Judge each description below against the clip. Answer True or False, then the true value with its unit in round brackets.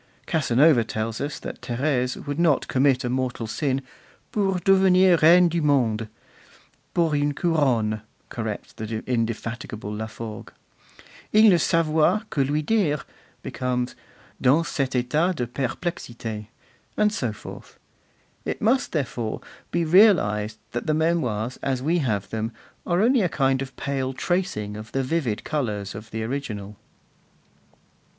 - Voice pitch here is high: False (135 Hz)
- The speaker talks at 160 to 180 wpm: False (135 wpm)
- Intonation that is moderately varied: False (6.4 semitones)